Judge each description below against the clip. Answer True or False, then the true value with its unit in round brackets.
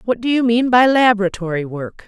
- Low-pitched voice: False (220 Hz)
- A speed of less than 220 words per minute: True (200 wpm)